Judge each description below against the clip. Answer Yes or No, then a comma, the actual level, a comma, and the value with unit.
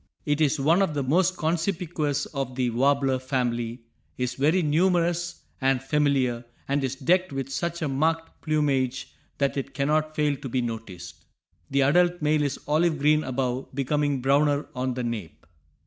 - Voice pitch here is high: No, medium, 140 Hz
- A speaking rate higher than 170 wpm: No, average, 165 wpm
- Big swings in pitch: No, average, 3.0 semitones